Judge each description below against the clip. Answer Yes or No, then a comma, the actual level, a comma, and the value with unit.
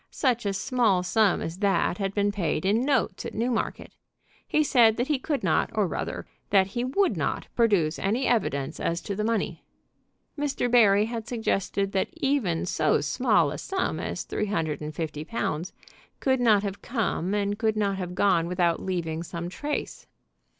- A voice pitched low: No, high, 205 Hz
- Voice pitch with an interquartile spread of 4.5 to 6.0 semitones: Yes, average, 5.0 semitones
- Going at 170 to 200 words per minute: Yes, average, 180 wpm